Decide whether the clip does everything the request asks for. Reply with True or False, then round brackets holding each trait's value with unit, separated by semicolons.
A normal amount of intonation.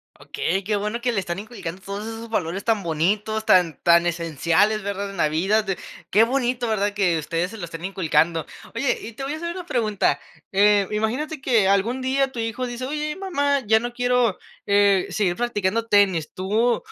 True (4.3 semitones)